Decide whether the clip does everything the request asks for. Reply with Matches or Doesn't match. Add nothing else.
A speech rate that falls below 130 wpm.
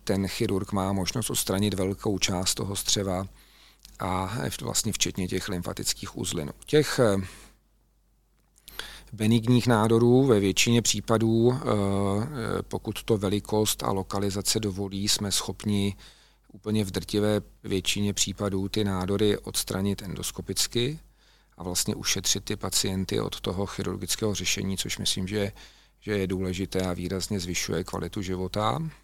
Matches